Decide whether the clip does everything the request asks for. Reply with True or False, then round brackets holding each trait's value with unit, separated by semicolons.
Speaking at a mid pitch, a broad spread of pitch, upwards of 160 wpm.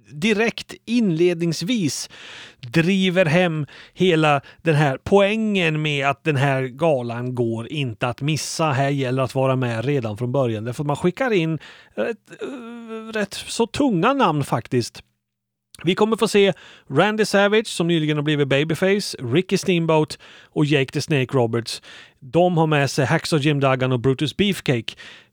False (155 Hz; 5.7 semitones; 150 wpm)